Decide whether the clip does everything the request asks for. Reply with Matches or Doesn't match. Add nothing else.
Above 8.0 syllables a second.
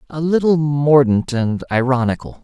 Doesn't match